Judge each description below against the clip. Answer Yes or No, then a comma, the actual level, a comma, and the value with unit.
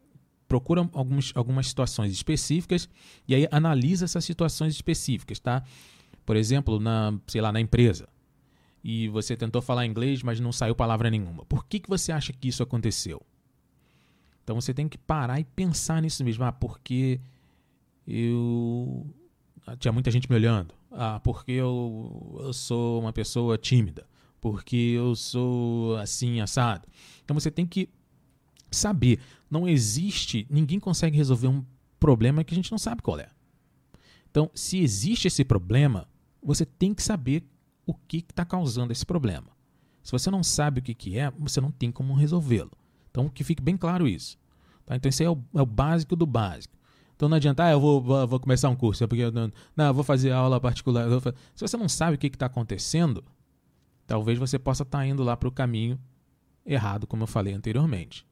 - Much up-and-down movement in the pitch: No, average, 4.5 semitones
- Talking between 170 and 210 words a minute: Yes, average, 180 wpm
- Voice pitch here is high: No, low, 130 Hz